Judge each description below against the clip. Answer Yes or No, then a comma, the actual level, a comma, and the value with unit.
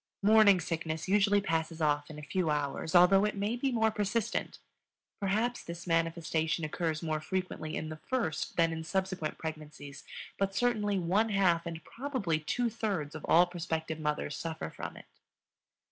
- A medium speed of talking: Yes, average, 160 wpm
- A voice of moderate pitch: Yes, medium, 170 Hz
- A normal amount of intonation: Yes, average, 4.3 semitones